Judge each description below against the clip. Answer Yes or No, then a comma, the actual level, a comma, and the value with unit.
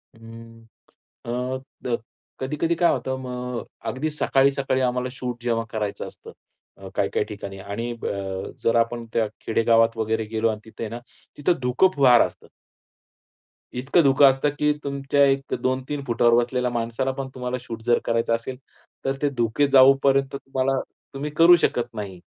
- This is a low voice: Yes, low, 125 Hz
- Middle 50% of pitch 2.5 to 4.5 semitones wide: Yes, average, 2.9 semitones